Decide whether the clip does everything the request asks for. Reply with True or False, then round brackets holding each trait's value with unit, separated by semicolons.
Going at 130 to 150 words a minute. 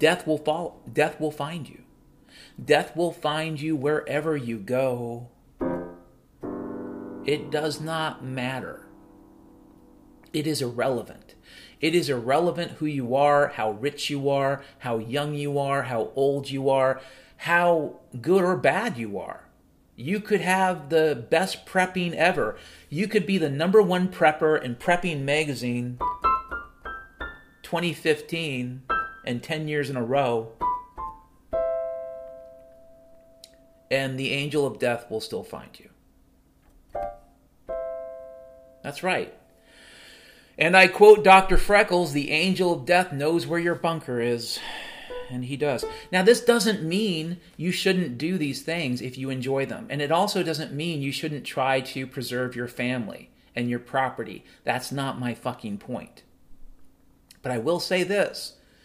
True (140 wpm)